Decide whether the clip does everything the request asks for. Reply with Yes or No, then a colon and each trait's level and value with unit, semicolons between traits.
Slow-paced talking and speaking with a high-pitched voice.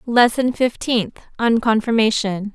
Yes: slow, 95 wpm; high, 230 Hz